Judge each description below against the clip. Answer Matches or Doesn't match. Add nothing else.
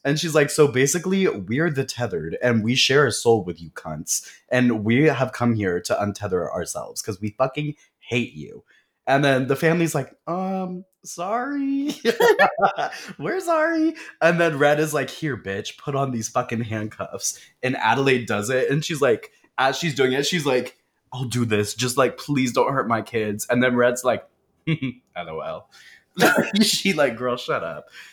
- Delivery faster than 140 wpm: Matches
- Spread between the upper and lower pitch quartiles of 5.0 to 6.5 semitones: Matches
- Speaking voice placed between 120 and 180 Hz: Matches